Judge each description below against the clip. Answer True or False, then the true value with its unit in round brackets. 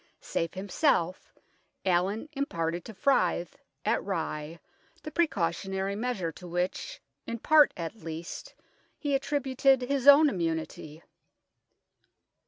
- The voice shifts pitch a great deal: True (8.2 semitones)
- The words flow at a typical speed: False (105 wpm)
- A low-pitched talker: False (195 Hz)